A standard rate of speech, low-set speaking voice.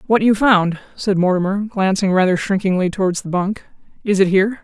No: average, 180 wpm; high, 195 Hz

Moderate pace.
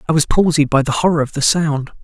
No: fast, 265 wpm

